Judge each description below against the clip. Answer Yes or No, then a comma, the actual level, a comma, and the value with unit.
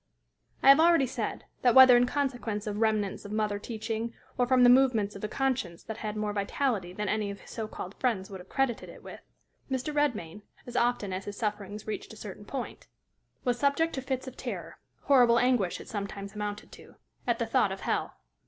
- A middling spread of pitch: Yes, average, 3.8 semitones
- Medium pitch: No, high, 220 Hz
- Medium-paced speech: No, fast, 210 wpm